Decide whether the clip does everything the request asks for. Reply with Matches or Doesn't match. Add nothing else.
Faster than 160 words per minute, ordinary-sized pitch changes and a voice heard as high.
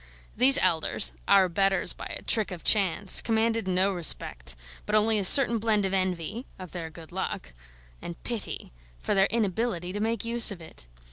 Matches